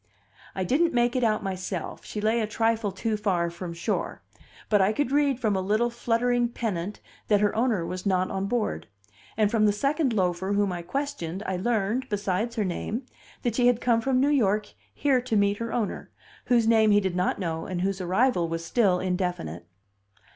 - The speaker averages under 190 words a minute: No, average, 195 wpm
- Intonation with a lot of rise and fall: No, average, 4.3 semitones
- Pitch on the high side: Yes, high, 210 Hz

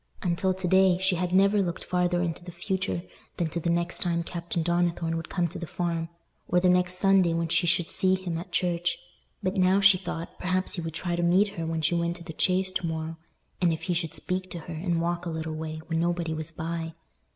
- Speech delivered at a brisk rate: Yes, fast, 235 wpm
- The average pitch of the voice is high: No, medium, 175 Hz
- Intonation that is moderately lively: No, narrow, 1.7 semitones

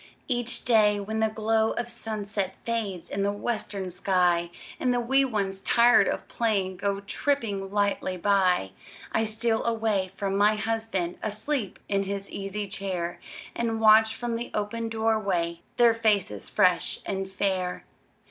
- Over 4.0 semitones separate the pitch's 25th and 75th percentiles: No, narrow, 2.6 semitones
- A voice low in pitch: No, high, 210 Hz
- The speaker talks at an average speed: Yes, average, 150 wpm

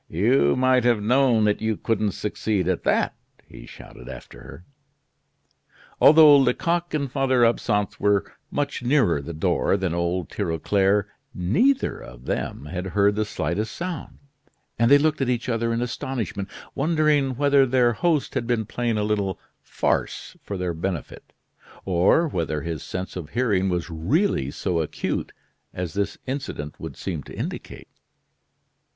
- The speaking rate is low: No, average, 150 wpm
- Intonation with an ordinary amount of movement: No, wide, 6.5 semitones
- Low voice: Yes, low, 105 Hz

